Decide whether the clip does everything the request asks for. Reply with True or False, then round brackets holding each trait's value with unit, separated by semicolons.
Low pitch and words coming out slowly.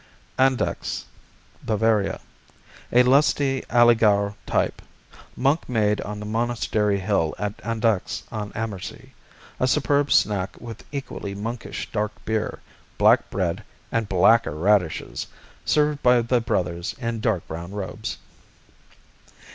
True (110 Hz; 115 wpm)